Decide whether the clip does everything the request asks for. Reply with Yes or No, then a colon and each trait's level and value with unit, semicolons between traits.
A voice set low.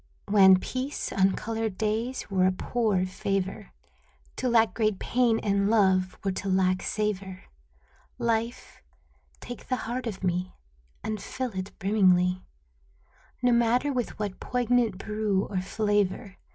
No: high, 210 Hz